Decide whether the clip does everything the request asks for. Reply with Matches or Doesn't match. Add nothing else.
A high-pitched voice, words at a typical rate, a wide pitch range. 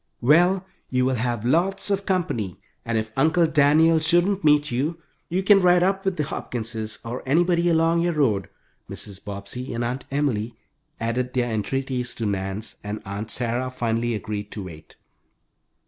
Doesn't match